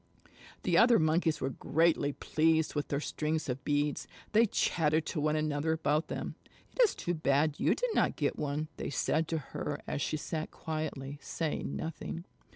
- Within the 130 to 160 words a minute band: No, average, 175 wpm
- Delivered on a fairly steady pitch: Yes, narrow, 1.7 semitones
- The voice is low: No, medium, 155 Hz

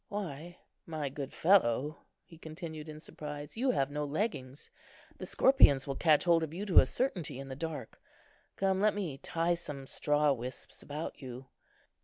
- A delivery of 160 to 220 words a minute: Yes, average, 170 wpm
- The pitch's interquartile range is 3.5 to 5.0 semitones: Yes, average, 4.0 semitones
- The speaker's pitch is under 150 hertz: No, medium, 155 Hz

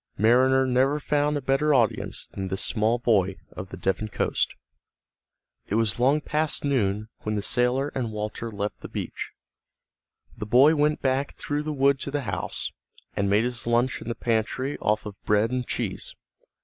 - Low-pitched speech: Yes, low, 120 Hz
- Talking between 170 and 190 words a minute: Yes, average, 175 wpm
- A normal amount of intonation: Yes, average, 4.4 semitones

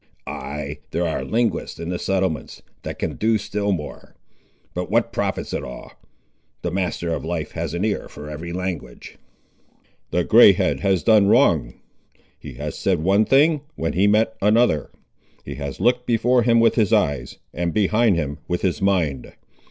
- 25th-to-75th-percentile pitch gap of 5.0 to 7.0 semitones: Yes, average, 5.3 semitones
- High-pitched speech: No, very low, 95 Hz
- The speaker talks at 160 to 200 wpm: Yes, average, 170 wpm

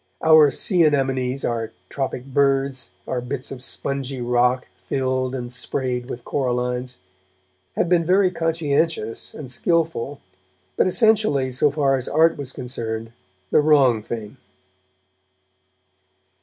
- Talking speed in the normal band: No, slow, 120 wpm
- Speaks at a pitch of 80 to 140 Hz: Yes, low, 135 Hz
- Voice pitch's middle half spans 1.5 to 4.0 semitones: Yes, average, 3.3 semitones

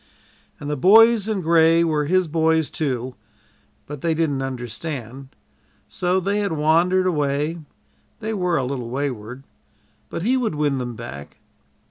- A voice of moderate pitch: Yes, medium, 155 Hz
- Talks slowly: No, average, 145 wpm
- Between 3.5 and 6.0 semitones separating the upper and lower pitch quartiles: Yes, average, 5.0 semitones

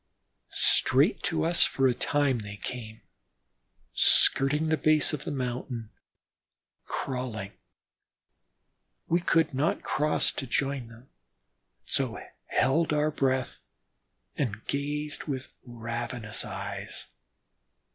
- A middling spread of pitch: Yes, average, 3.7 semitones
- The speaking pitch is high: No, low, 135 Hz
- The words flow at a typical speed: No, slow, 105 wpm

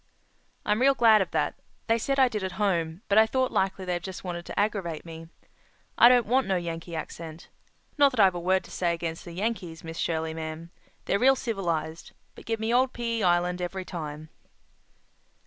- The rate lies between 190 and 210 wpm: Yes, average, 200 wpm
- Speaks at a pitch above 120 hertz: Yes, medium, 185 Hz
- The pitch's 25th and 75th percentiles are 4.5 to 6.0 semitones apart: Yes, average, 5.0 semitones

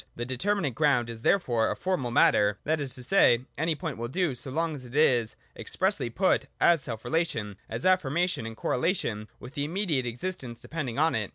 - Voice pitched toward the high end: No, low, 135 Hz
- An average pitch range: No, wide, 5.8 semitones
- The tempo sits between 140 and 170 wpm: No, average, 195 wpm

